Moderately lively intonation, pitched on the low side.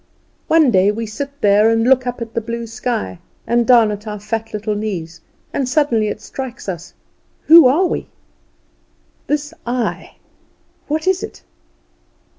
No: average, 4.0 semitones; high, 230 Hz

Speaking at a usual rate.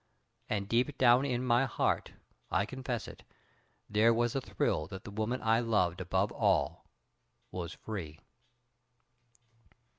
No: slow, 130 wpm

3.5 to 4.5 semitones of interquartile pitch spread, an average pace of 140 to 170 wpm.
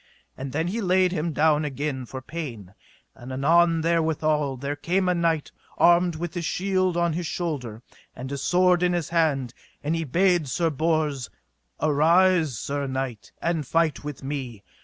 Yes: average, 3.8 semitones; average, 165 wpm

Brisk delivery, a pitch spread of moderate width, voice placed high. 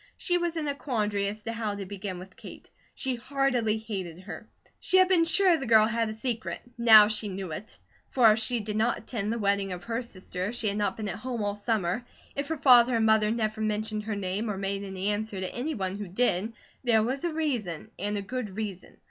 Yes: fast, 235 wpm; average, 3.3 semitones; high, 215 Hz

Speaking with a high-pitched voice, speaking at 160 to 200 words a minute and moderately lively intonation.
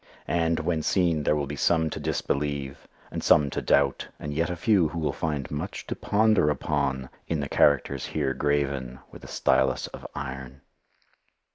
No: very low, 75 Hz; average, 175 wpm; average, 3.0 semitones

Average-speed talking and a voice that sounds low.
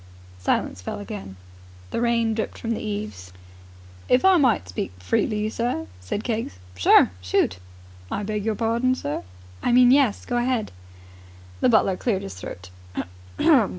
No: average, 150 wpm; high, 215 Hz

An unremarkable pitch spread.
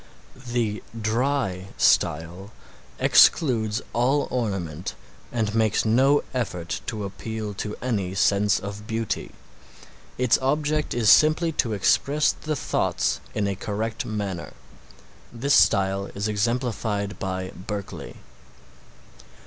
Yes: average, 3.7 semitones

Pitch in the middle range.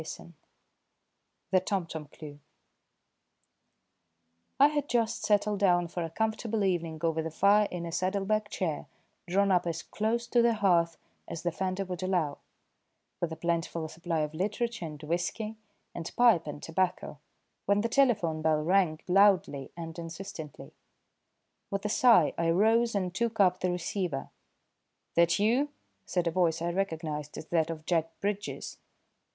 Yes: medium, 180 Hz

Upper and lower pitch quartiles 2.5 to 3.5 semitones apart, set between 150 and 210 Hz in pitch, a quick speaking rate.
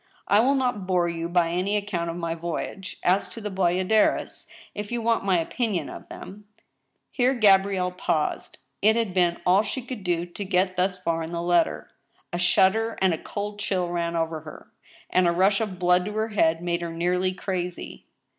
Yes: average, 3.1 semitones; medium, 185 Hz; fast, 210 wpm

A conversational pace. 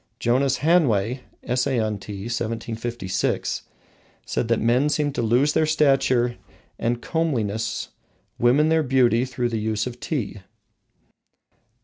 No: slow, 120 wpm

